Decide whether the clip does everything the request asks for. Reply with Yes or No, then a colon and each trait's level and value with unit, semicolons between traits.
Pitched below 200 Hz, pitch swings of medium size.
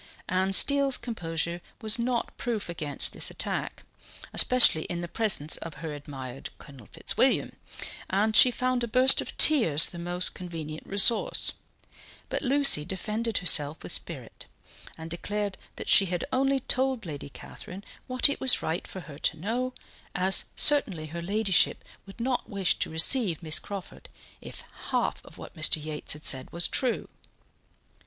No: high, 190 Hz; wide, 6.7 semitones